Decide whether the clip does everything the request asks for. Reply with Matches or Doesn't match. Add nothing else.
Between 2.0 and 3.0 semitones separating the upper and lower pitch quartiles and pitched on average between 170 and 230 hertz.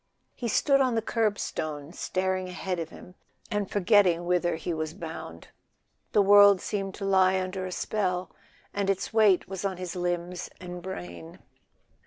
Matches